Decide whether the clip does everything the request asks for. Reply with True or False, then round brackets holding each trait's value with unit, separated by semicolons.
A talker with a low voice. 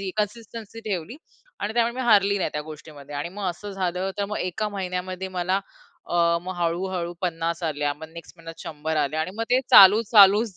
False (185 Hz)